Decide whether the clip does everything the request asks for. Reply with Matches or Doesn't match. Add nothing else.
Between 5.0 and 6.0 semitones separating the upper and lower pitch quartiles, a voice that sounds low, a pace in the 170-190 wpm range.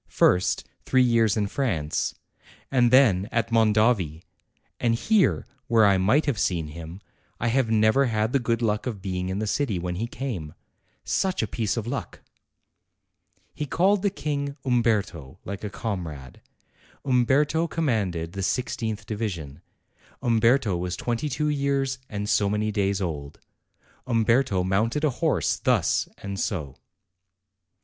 Doesn't match